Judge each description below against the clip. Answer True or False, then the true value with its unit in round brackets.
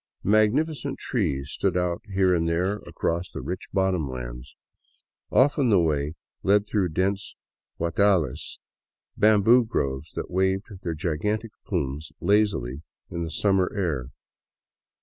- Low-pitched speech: True (90 Hz)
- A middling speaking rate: False (125 wpm)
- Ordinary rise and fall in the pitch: True (4.9 semitones)